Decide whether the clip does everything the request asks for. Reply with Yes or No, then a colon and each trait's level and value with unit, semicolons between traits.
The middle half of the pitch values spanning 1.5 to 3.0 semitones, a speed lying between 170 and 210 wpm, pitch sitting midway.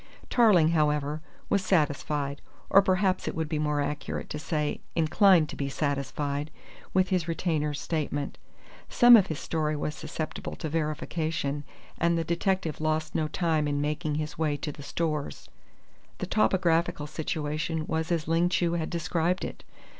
No: narrow, 2.4 semitones; average, 155 wpm; medium, 155 Hz